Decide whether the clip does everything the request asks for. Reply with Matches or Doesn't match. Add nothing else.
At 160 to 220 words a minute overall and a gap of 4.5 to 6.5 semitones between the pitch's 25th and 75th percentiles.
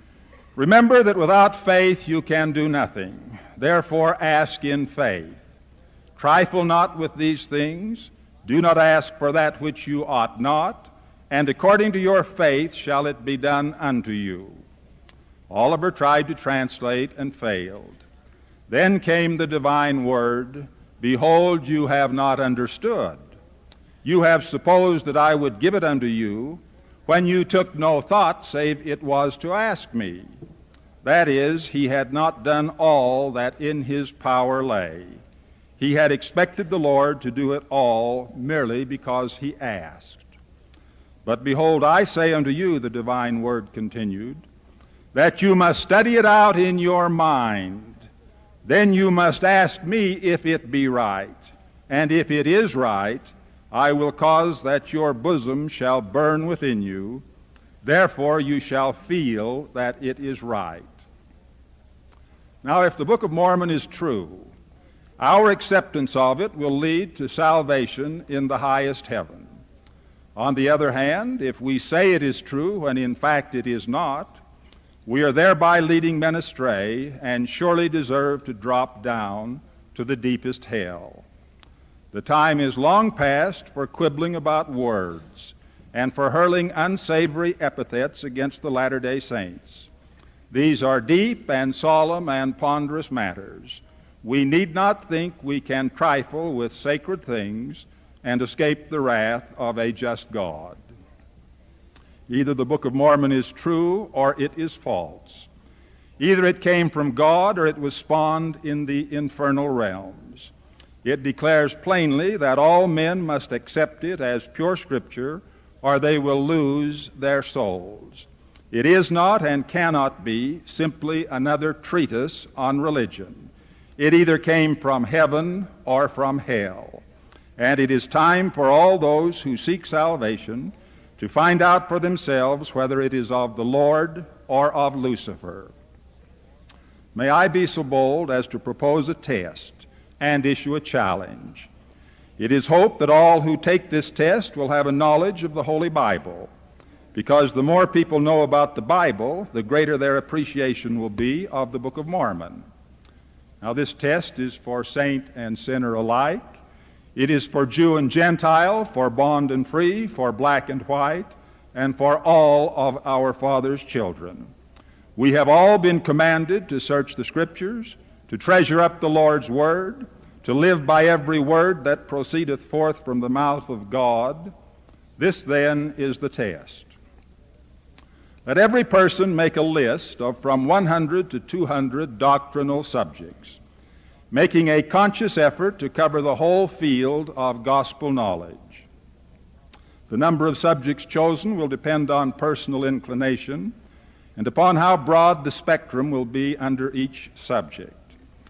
Doesn't match